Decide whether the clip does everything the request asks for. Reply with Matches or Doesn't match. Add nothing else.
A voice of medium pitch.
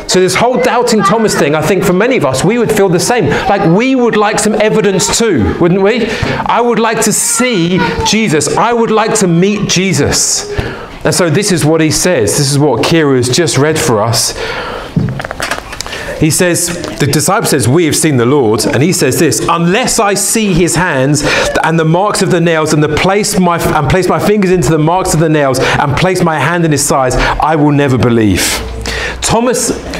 Matches